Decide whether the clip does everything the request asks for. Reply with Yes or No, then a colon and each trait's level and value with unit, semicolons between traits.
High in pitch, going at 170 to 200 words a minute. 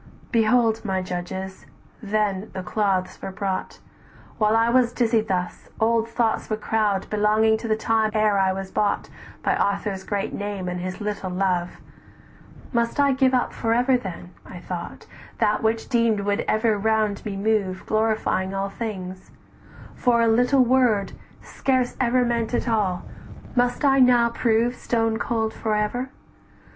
No: high, 215 Hz; average, 160 wpm